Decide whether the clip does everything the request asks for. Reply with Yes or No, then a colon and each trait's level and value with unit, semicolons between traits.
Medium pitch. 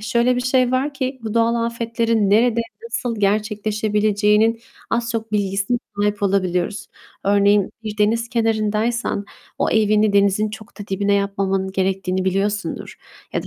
No: high, 210 Hz